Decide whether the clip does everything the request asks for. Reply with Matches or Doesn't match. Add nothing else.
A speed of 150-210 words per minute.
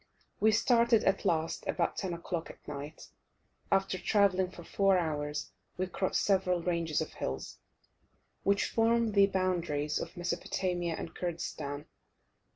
Doesn't match